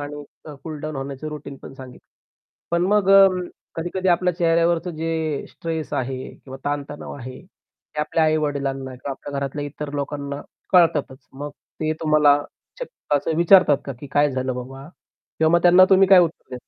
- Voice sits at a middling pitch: Yes, medium, 150 Hz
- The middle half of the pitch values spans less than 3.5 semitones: Yes, average, 3.1 semitones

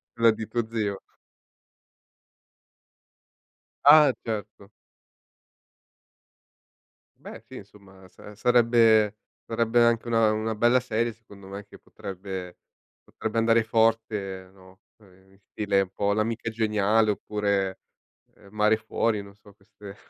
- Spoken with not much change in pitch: Yes, narrow, 2.3 semitones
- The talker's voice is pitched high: No, low, 110 Hz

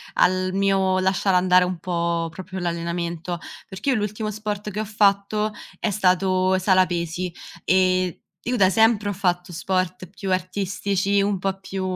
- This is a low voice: No, medium, 185 Hz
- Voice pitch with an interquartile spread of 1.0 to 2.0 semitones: Yes, narrow, 1.7 semitones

